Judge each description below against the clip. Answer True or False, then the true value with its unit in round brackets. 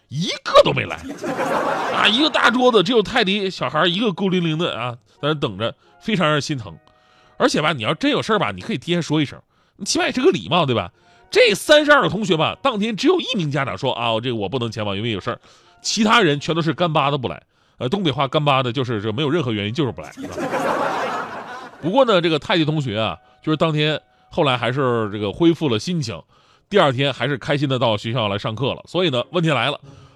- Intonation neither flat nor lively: False (6.7 semitones)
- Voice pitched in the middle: True (150 Hz)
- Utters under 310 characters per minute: False (340 characters per minute)